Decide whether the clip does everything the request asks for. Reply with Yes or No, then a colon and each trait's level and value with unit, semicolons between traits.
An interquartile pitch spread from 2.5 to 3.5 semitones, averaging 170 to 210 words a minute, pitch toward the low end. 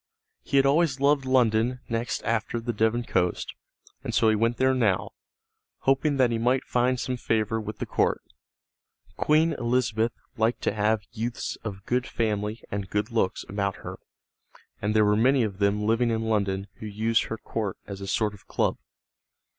Yes: average, 2.9 semitones; average, 180 wpm; low, 115 Hz